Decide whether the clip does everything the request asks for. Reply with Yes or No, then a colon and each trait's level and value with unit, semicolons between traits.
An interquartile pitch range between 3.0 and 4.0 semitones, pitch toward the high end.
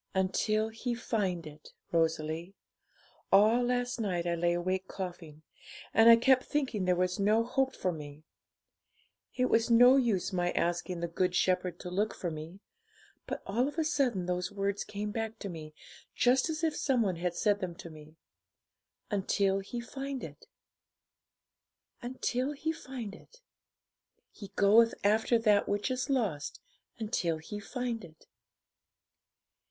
No: wide, 5.4 semitones; high, 205 Hz